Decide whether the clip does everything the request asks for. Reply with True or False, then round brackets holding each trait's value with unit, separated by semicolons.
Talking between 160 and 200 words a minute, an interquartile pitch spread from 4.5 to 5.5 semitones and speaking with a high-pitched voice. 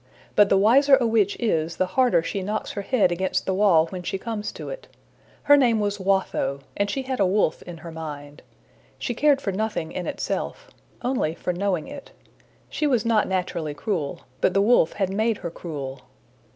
True (195 wpm; 5.1 semitones; 195 Hz)